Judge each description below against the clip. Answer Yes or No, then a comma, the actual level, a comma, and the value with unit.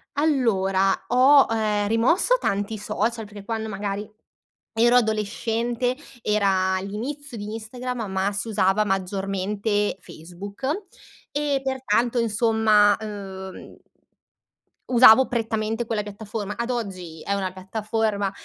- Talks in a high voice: Yes, high, 215 Hz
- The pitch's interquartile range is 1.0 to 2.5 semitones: No, average, 2.9 semitones